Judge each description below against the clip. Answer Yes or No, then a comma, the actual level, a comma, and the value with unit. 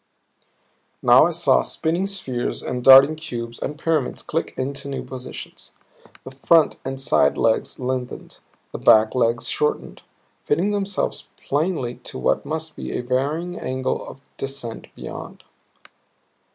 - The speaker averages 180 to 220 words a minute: No, slow, 135 wpm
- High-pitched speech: No, low, 135 Hz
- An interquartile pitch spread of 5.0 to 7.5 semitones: No, average, 4.1 semitones